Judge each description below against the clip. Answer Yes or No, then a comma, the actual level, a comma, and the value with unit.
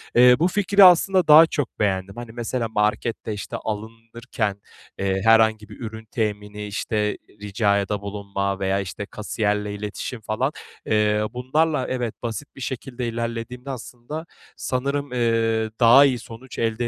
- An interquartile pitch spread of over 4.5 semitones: No, average, 3.2 semitones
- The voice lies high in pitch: No, low, 115 Hz